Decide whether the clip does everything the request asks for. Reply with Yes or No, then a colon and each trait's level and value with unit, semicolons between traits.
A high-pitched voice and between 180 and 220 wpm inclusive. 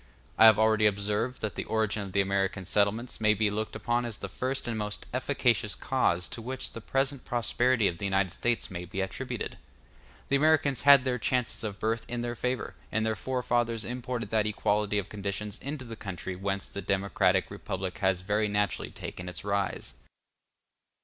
No: low, 105 Hz; average, 185 wpm